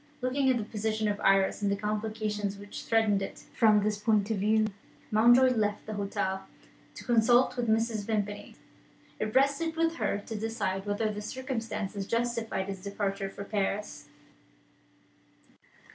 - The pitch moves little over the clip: Yes, narrow, 2.2 semitones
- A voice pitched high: Yes, high, 215 Hz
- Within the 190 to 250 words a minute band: No, average, 155 wpm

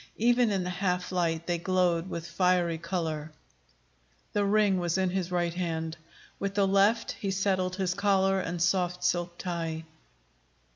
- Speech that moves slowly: No, average, 155 wpm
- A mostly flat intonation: Yes, narrow, 2.1 semitones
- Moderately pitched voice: Yes, medium, 180 Hz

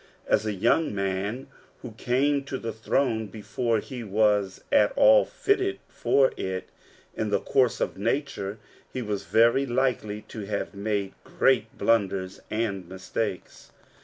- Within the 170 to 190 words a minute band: No, average, 140 wpm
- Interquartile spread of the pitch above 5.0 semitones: No, average, 4.6 semitones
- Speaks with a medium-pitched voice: No, low, 110 Hz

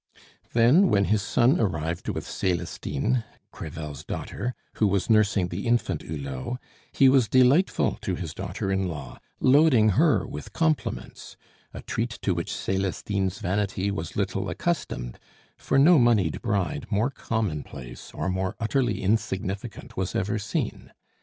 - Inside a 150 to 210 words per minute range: No, average, 140 wpm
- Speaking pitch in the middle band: No, low, 100 Hz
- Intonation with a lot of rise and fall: No, average, 5.0 semitones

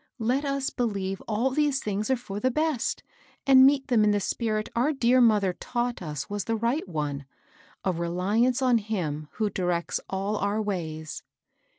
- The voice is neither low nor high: No, high, 215 Hz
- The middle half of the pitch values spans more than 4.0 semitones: Yes, average, 4.9 semitones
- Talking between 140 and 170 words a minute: No, average, 180 wpm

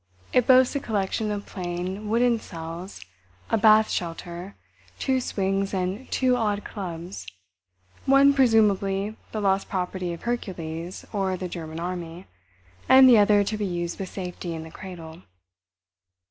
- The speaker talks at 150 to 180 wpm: No, average, 140 wpm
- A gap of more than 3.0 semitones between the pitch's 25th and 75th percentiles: Yes, average, 3.8 semitones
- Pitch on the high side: Yes, high, 195 Hz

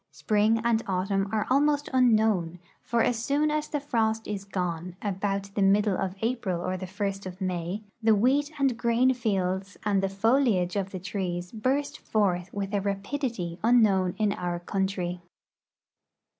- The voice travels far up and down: No, average, 3.6 semitones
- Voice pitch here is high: Yes, high, 200 Hz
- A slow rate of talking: No, average, 160 wpm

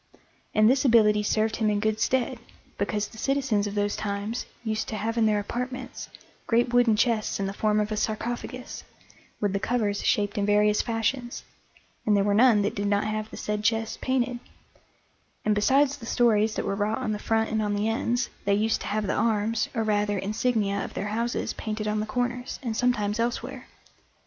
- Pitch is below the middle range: No, high, 215 Hz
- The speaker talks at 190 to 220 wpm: Yes, average, 200 wpm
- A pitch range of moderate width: No, narrow, 2.3 semitones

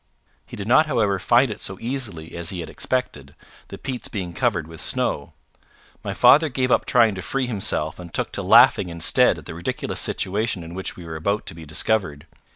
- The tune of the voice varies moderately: No, wide, 6.3 semitones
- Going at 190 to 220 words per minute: Yes, fast, 205 wpm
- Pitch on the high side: No, very low, 95 Hz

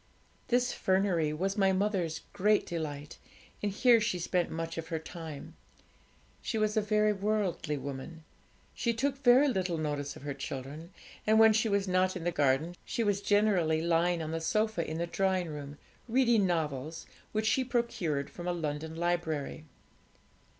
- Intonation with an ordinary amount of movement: Yes, average, 5.0 semitones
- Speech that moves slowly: No, average, 165 wpm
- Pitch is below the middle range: No, medium, 175 Hz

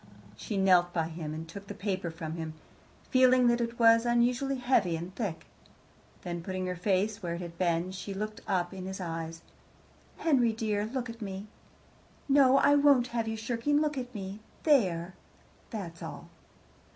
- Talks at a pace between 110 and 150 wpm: No, average, 175 wpm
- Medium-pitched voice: No, high, 200 Hz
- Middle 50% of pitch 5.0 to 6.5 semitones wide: Yes, wide, 5.4 semitones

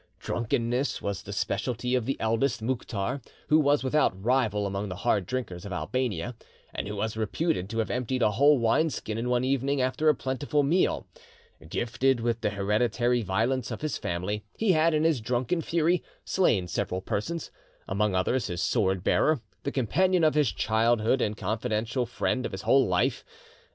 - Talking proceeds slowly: No, average, 175 wpm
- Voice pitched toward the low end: Yes, low, 120 Hz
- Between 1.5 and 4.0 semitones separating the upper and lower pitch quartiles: No, average, 4.6 semitones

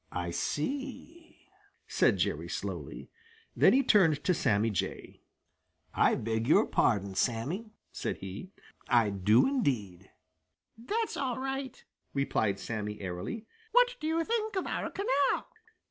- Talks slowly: Yes, slow, 130 wpm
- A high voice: No, medium, 150 Hz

